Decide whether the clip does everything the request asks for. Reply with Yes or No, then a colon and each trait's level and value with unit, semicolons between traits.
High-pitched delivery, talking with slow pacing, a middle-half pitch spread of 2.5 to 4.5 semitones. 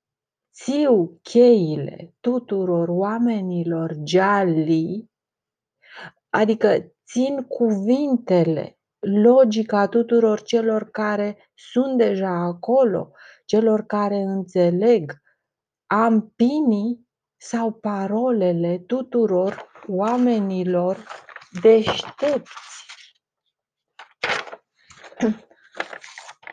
Yes: high, 215 Hz; slow, 55 wpm; average, 4.2 semitones